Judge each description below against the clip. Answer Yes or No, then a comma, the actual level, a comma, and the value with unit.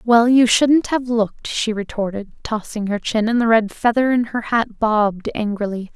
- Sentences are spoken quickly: No, average, 190 wpm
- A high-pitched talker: Yes, high, 225 Hz